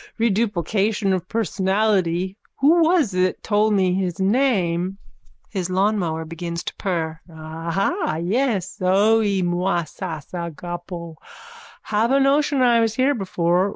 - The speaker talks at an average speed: No, slow, 120 wpm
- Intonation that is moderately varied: Yes, average, 4.3 semitones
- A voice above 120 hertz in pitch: Yes, high, 190 Hz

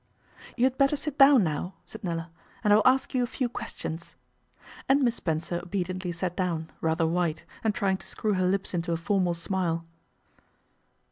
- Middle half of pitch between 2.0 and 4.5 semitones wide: No, average, 4.9 semitones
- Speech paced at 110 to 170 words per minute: No, average, 185 wpm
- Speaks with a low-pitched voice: No, medium, 185 Hz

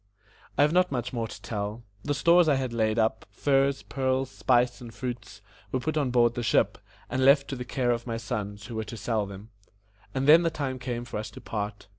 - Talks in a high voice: No, low, 120 Hz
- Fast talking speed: Yes, fast, 230 wpm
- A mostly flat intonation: No, average, 3.3 semitones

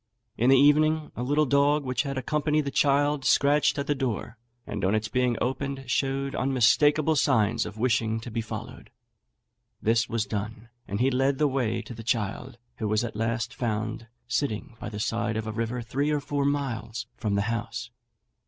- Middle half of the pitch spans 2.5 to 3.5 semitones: No, average, 3.9 semitones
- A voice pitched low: Yes, low, 125 Hz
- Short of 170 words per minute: No, average, 190 wpm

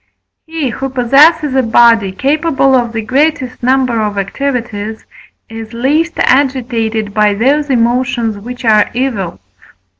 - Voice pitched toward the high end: Yes, high, 245 Hz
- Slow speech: Yes, slow, 130 wpm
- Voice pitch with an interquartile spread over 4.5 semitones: No, average, 3.4 semitones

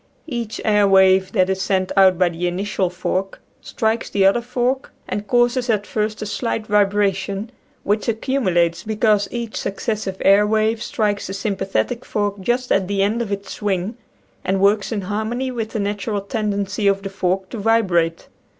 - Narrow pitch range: Yes, narrow, 2.3 semitones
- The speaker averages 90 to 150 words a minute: No, average, 180 wpm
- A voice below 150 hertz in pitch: No, high, 205 Hz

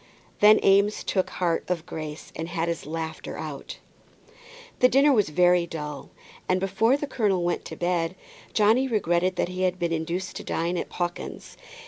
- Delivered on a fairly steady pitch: No, average, 3.2 semitones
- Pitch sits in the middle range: Yes, medium, 180 Hz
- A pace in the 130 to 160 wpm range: No, average, 170 wpm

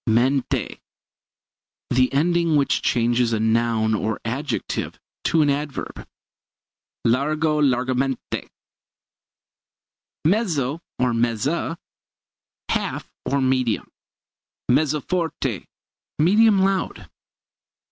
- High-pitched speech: No, low, 135 Hz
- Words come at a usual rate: No, slow, 80 wpm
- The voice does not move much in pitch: No, average, 4.7 semitones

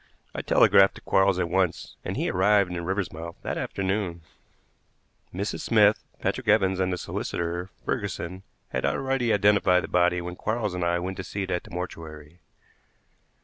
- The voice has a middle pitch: No, very low, 95 Hz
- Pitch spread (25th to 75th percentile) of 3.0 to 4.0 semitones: No, narrow, 2.4 semitones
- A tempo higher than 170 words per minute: No, average, 165 wpm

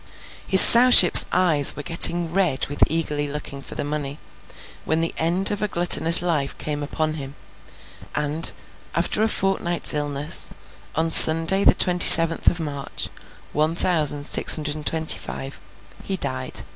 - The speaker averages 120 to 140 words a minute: No, average, 155 wpm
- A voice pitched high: No, medium, 160 Hz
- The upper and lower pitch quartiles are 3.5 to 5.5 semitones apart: No, average, 2.9 semitones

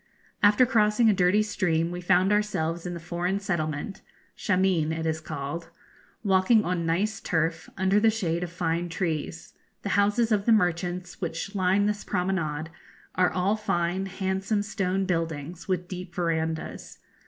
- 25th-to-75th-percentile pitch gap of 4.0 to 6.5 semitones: No, average, 3.3 semitones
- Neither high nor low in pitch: Yes, medium, 180 Hz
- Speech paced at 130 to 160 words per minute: Yes, average, 155 wpm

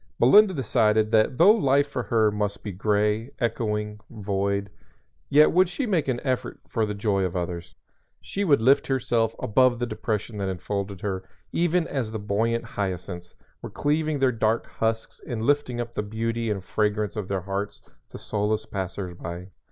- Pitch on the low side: Yes, low, 110 Hz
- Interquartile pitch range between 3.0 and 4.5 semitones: Yes, average, 4.0 semitones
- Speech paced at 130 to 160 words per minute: No, average, 175 wpm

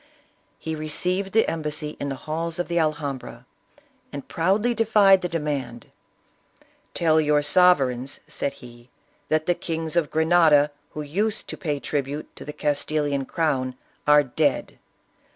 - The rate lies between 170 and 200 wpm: No, average, 150 wpm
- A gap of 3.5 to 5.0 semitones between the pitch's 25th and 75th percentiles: No, average, 3.1 semitones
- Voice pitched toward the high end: No, medium, 155 Hz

